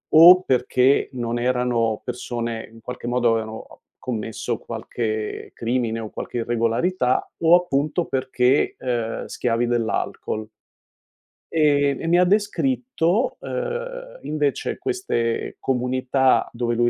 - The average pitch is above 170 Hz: No, low, 125 Hz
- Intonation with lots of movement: Yes, wide, 5.8 semitones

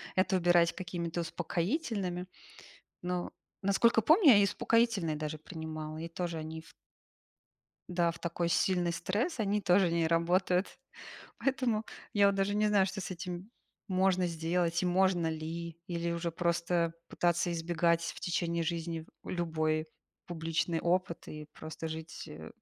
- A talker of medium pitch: Yes, medium, 175 Hz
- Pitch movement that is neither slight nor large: No, narrow, 2.2 semitones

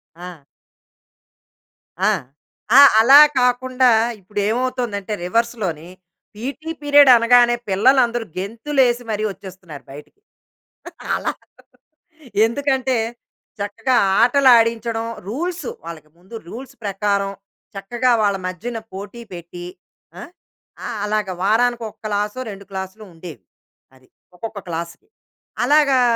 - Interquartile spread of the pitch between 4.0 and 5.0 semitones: Yes, average, 4.4 semitones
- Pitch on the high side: Yes, high, 225 Hz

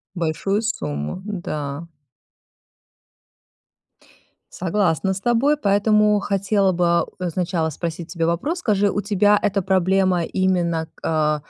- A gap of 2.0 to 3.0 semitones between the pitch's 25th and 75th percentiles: No, average, 3.5 semitones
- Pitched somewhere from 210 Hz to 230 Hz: No, medium, 185 Hz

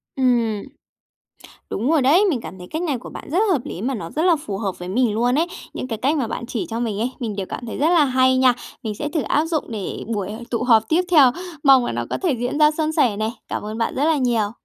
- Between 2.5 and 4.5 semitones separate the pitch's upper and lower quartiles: No, average, 5.2 semitones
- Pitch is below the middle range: No, high, 245 Hz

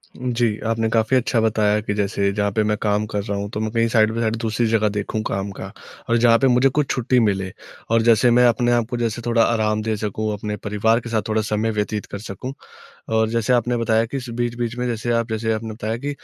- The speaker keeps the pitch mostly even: Yes, narrow, 1.9 semitones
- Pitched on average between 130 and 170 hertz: No, low, 110 Hz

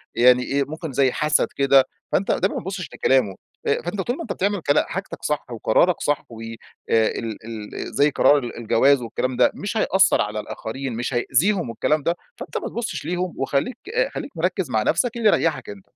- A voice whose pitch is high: No, medium, 140 Hz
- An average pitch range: No, wide, 7.2 semitones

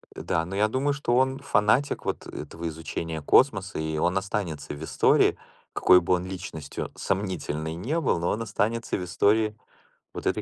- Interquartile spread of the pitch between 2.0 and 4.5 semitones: No, average, 5.2 semitones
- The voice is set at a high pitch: No, very low, 95 Hz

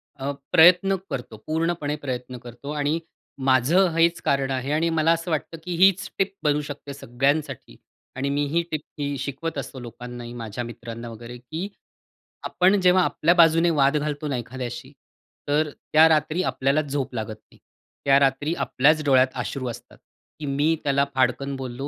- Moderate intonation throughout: Yes, average, 3.7 semitones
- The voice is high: No, medium, 140 Hz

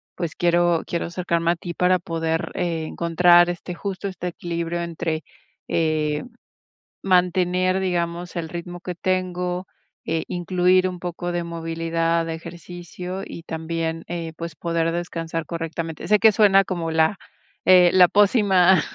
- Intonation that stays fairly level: Yes, narrow, 1.5 semitones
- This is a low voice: No, medium, 175 Hz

